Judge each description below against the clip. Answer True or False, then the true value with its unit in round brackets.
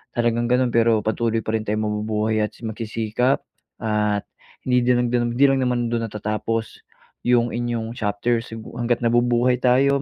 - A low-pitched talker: True (115 Hz)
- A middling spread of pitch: False (1.9 semitones)